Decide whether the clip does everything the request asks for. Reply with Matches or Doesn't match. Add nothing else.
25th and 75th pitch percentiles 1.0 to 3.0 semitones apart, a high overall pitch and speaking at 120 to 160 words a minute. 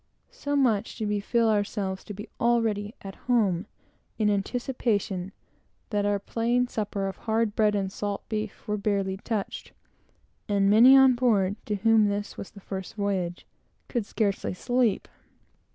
Matches